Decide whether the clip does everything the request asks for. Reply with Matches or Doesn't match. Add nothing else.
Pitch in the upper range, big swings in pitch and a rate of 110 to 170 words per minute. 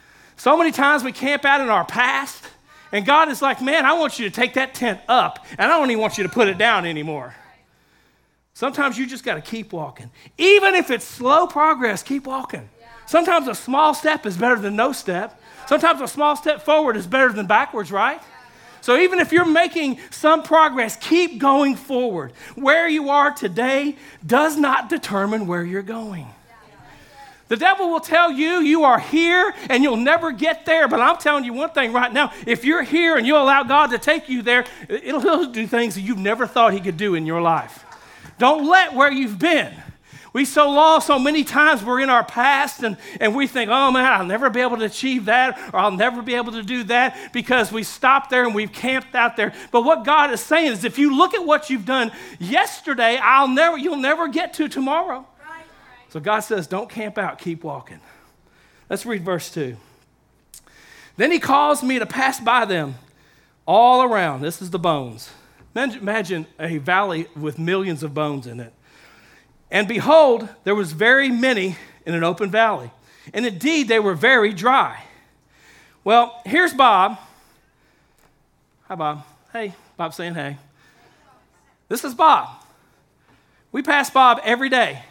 Doesn't match